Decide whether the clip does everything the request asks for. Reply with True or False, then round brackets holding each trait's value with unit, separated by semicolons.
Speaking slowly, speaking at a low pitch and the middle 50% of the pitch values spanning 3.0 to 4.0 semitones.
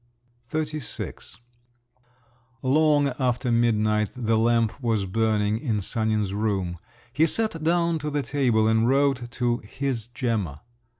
False (120 wpm; 120 Hz; 4.5 semitones)